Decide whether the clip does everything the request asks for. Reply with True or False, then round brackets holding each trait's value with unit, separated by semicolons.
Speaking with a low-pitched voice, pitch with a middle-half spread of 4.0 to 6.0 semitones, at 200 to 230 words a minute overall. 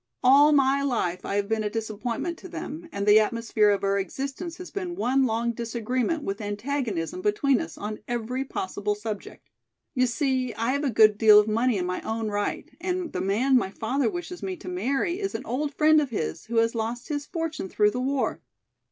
False (235 Hz; 5.1 semitones; 205 wpm)